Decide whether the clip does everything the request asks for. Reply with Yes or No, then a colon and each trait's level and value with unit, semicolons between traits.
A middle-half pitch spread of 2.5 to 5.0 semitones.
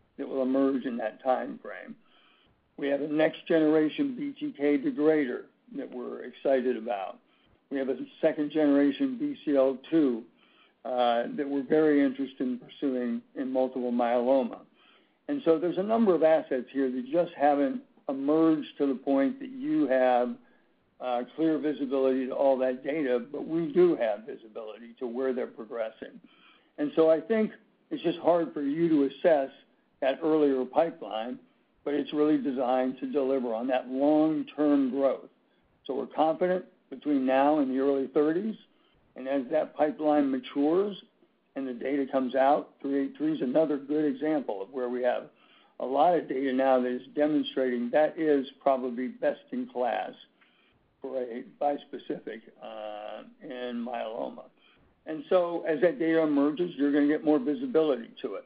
Yes: average, 3.5 semitones